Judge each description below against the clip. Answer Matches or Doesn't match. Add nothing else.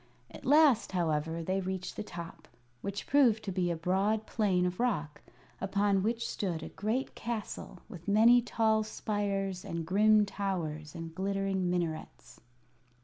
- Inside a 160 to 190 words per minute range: Doesn't match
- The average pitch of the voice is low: Doesn't match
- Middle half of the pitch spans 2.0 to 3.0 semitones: Doesn't match